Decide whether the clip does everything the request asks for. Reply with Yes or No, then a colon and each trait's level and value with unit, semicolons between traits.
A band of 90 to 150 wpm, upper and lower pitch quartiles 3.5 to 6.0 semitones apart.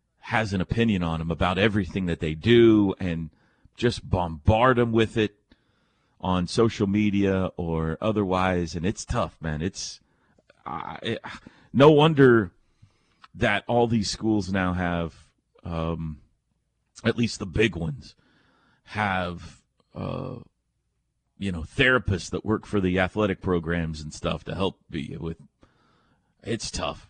Yes: slow, 135 wpm; average, 4.3 semitones